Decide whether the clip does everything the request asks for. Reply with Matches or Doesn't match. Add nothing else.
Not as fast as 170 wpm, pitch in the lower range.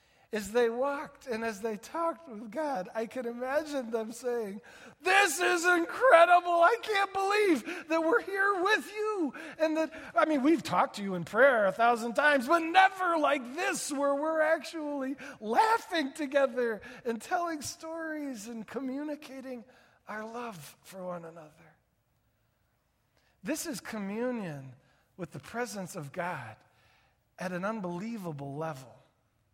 Doesn't match